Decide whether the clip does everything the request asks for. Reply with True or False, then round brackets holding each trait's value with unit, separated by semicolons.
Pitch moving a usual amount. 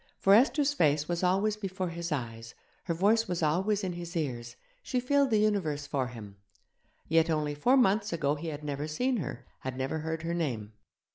False (5.7 semitones)